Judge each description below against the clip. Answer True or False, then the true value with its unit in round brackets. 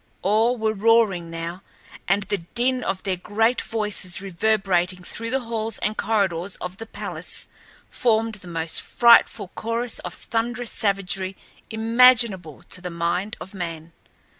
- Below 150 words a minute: True (140 wpm)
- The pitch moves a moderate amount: True (3.9 semitones)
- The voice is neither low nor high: False (205 Hz)